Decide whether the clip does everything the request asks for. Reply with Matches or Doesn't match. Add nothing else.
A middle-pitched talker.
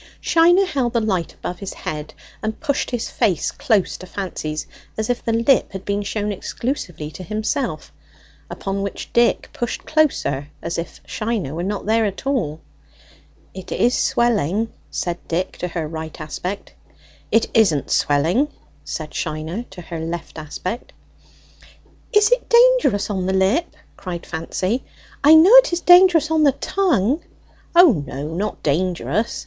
Doesn't match